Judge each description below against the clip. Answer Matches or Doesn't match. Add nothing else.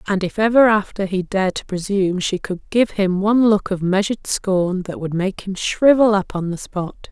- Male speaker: Doesn't match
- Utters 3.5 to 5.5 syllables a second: Matches